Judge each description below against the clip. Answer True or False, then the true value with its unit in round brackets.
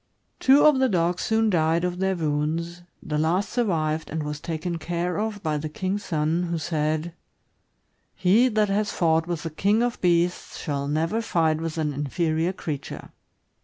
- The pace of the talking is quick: False (175 wpm)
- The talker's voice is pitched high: False (170 Hz)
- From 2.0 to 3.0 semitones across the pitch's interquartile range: False (3.5 semitones)